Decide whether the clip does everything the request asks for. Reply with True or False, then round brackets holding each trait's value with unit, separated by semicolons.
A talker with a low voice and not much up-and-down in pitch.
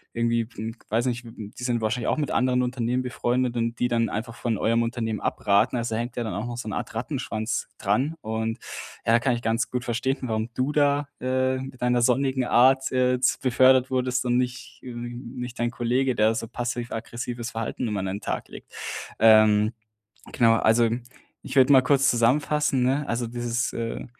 True (120 Hz; 1.9 semitones)